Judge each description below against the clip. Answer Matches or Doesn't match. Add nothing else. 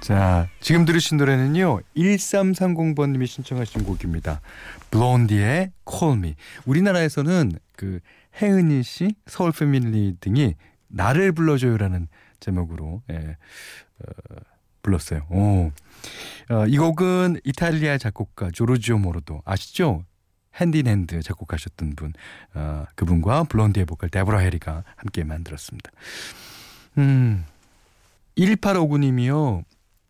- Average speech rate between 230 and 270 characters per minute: Matches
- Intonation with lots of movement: Matches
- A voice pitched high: Doesn't match